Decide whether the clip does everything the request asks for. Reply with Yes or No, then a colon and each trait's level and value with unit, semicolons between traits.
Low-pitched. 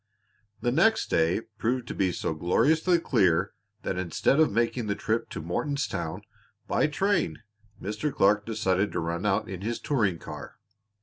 Yes: low, 105 Hz